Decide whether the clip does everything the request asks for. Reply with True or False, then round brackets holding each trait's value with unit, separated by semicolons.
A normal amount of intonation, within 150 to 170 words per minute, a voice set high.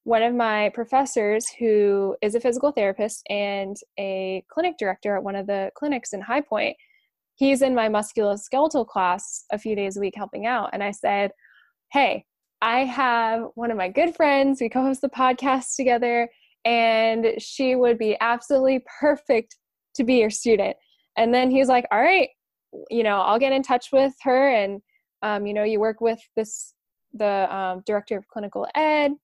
False (4.2 semitones; 180 wpm; 230 Hz)